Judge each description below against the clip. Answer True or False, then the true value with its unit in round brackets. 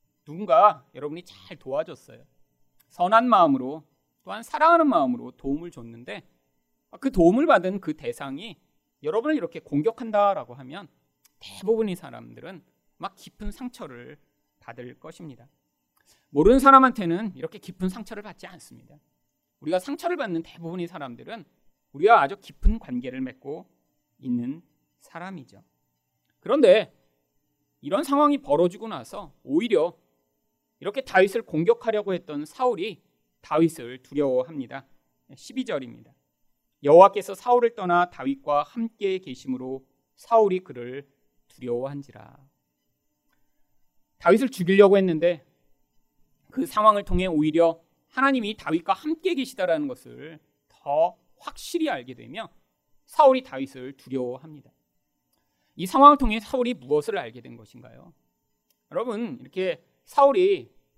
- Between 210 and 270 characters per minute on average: False (290 characters per minute)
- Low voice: False (170 Hz)